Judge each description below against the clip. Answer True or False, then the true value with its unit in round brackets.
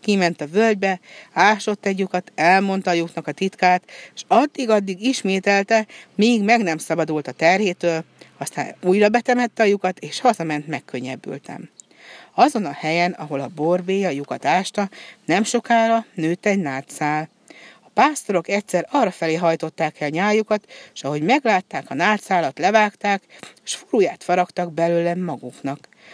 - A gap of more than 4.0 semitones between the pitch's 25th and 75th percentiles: True (4.6 semitones)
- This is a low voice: False (185 Hz)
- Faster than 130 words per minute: True (140 wpm)